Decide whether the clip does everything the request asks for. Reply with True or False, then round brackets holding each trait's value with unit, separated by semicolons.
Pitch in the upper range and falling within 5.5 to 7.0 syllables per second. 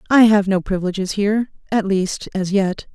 False (200 Hz; 5.3 syllables/s)